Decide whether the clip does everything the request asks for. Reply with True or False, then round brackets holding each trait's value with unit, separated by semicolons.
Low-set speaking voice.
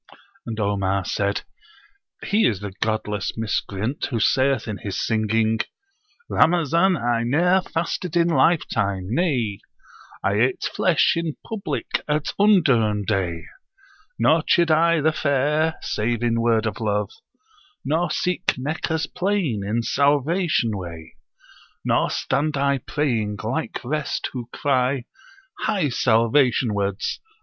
True (125 Hz)